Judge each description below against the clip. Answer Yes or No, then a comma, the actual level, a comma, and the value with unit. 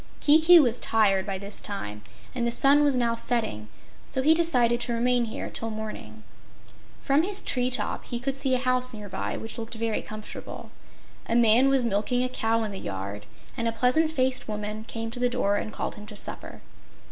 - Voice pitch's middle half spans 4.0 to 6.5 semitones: No, average, 3.0 semitones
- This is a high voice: Yes, high, 235 Hz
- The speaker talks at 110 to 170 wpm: No, fast, 205 wpm